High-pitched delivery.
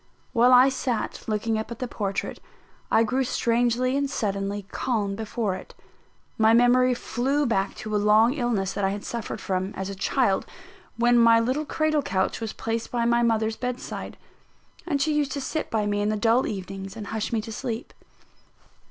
Yes: high, 230 Hz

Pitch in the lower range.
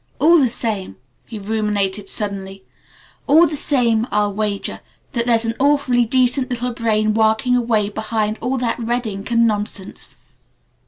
No: high, 225 Hz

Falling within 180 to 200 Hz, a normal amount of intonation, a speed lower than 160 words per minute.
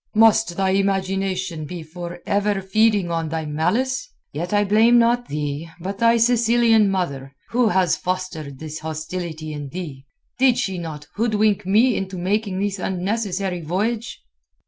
Yes: high, 190 Hz; average, 4.6 semitones; average, 145 wpm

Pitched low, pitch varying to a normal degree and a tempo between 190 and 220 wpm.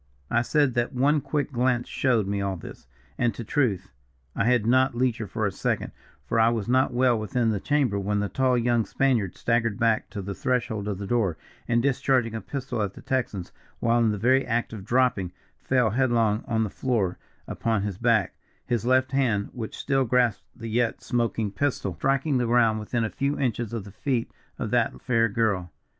Yes: low, 115 Hz; average, 3.2 semitones; average, 200 wpm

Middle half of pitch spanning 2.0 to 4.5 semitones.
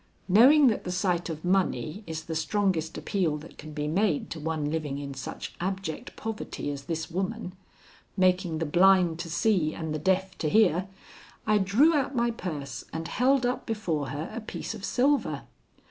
No: average, 4.9 semitones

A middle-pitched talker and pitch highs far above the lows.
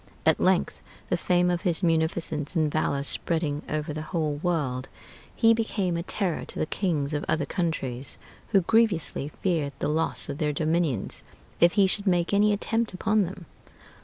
No: medium, 165 Hz; average, 3.8 semitones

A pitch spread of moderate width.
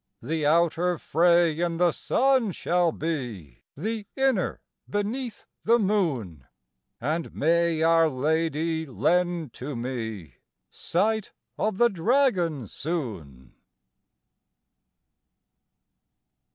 Yes: average, 4.8 semitones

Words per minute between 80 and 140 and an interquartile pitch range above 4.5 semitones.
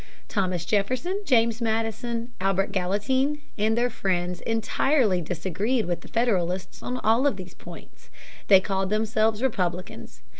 No: slow, 135 wpm; average, 4.1 semitones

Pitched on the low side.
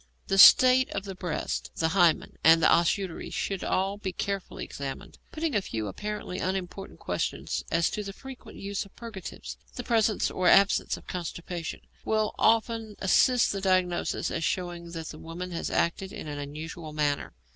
No: medium, 185 Hz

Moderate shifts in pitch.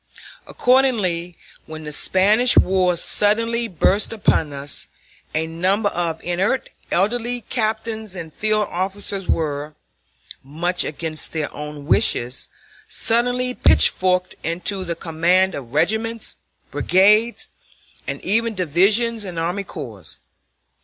Yes: average, 5.0 semitones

